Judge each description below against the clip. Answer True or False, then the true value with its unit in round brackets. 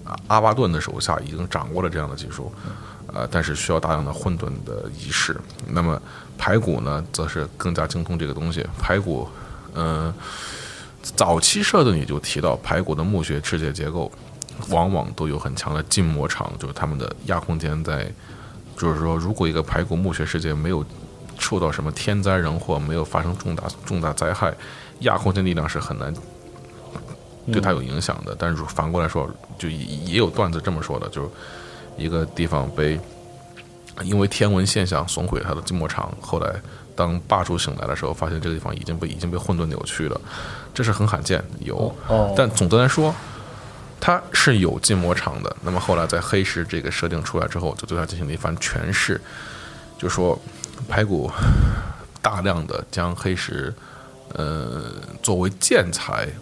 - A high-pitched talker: False (85 Hz)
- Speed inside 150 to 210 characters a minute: False (265 characters per minute)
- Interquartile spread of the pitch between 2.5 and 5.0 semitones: True (3.8 semitones)